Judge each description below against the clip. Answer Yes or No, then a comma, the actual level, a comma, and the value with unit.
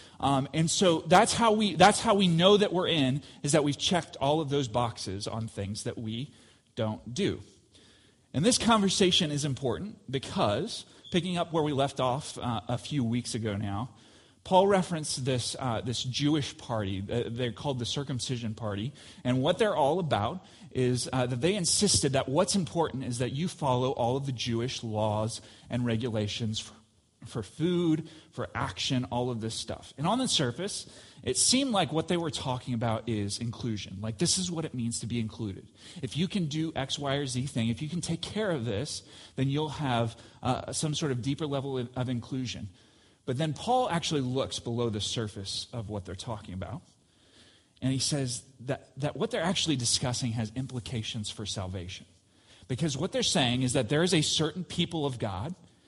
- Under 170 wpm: No, average, 195 wpm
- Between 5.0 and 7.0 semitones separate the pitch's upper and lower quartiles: Yes, wide, 5.6 semitones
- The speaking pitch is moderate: No, low, 130 Hz